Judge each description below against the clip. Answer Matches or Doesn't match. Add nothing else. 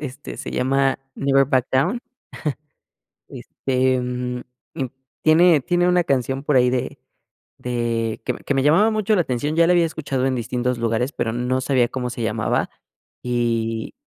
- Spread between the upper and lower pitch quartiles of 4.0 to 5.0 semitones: Doesn't match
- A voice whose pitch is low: Matches